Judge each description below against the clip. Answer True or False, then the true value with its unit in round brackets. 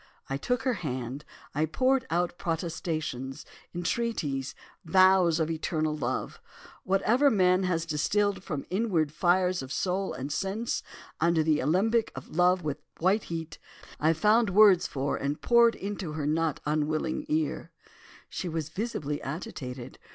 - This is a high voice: False (170 Hz)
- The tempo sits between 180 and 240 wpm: False (145 wpm)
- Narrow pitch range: False (4.5 semitones)